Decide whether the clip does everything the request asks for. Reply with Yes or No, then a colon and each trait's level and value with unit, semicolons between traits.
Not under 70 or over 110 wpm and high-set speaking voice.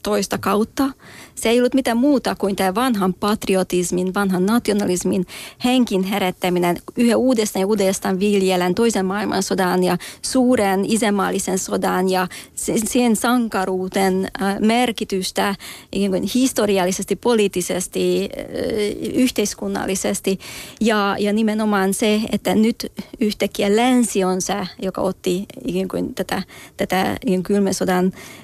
Yes: average, 105 wpm; high, 200 Hz